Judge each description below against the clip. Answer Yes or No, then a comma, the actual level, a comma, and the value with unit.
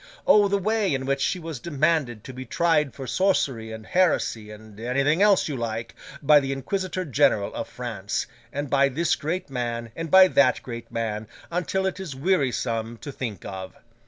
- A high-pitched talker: No, low, 135 Hz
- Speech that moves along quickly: No, average, 185 wpm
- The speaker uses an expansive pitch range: Yes, wide, 6.5 semitones